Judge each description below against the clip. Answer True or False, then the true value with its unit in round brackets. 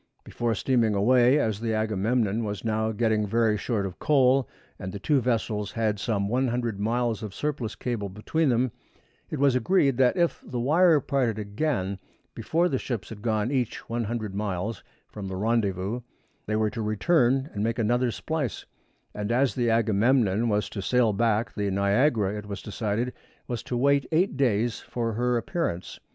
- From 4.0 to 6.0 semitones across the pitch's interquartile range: False (3.3 semitones)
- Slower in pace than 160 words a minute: False (170 wpm)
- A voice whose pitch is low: True (115 Hz)